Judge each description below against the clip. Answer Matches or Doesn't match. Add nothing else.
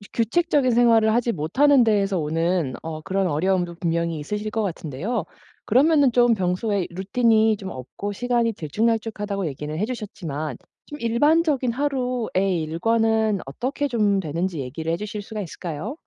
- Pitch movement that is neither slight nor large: Doesn't match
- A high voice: Matches